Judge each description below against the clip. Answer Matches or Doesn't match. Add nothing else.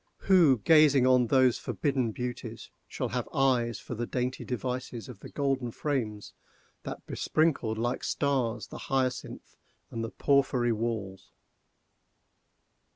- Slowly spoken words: Matches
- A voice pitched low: Matches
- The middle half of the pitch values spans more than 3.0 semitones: Doesn't match